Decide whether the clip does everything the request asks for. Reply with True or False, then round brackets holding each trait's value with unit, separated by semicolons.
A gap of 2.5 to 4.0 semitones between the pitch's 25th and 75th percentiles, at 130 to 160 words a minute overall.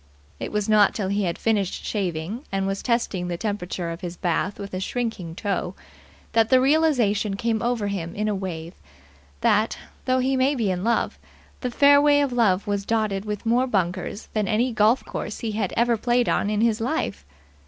False (3.6 semitones; 195 wpm)